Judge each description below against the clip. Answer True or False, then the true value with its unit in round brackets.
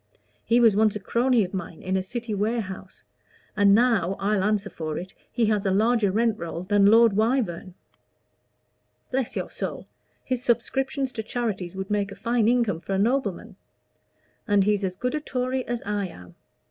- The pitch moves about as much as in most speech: True (3.7 semitones)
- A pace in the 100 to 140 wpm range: False (180 wpm)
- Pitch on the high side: True (210 Hz)